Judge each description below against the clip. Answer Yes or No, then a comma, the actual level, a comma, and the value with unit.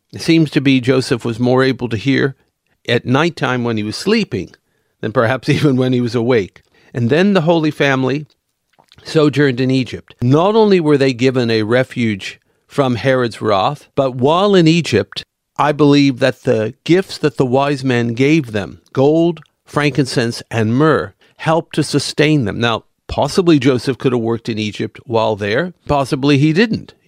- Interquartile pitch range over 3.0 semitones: Yes, average, 3.7 semitones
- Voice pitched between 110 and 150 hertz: Yes, low, 135 Hz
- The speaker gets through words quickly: No, average, 170 wpm